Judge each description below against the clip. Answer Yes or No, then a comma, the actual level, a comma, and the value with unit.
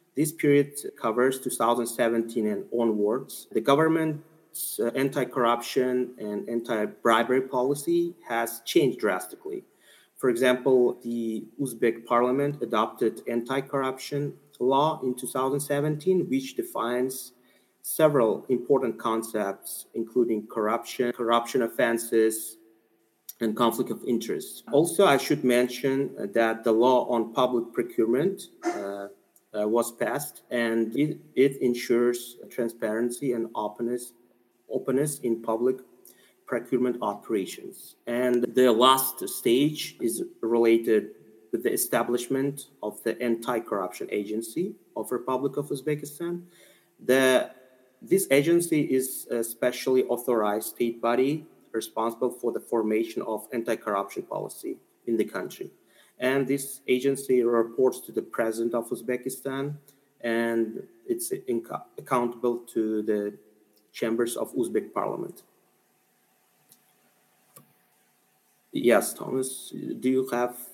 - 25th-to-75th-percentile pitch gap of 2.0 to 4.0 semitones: Yes, average, 3.0 semitones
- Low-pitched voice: Yes, low, 125 Hz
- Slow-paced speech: Yes, slow, 105 wpm